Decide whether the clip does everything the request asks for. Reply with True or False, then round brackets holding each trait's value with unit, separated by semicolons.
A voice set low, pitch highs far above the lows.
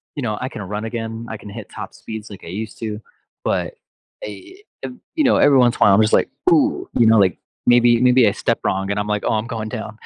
False (110 Hz; 2.7 semitones)